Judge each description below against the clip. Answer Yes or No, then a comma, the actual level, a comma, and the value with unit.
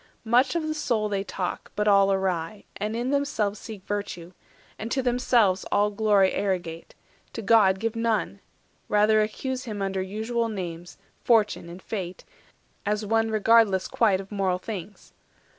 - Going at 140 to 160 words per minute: Yes, average, 155 wpm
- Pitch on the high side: Yes, high, 210 Hz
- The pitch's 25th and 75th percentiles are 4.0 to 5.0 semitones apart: No, average, 2.9 semitones